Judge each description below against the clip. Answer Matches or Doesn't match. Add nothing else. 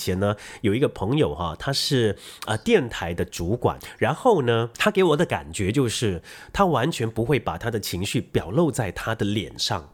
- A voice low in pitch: Matches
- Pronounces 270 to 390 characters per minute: Matches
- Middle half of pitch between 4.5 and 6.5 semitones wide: Matches